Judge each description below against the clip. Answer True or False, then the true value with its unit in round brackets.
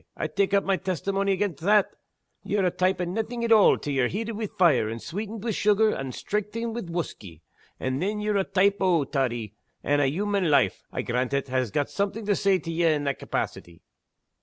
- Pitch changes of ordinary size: False (6.7 semitones)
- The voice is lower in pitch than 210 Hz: True (185 Hz)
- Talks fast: True (210 wpm)